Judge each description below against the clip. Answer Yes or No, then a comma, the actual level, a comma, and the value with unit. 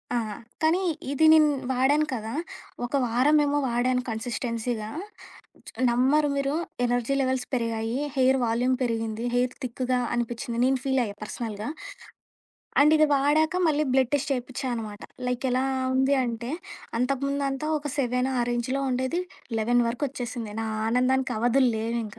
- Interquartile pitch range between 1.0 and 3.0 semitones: Yes, narrow, 2.6 semitones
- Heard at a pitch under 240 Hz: No, very high, 250 Hz